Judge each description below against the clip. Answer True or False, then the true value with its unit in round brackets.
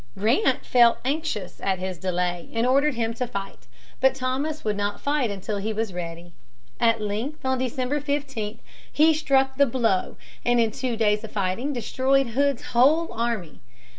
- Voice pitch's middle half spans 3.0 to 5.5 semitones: True (4.7 semitones)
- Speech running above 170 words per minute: False (165 wpm)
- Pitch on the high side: True (235 Hz)